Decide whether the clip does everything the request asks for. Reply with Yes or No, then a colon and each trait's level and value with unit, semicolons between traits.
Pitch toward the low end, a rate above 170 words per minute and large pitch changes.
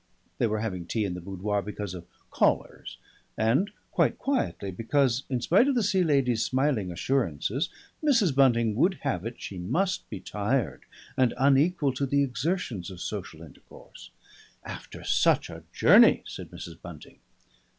No: low, 120 Hz; average, 155 wpm; wide, 6.4 semitones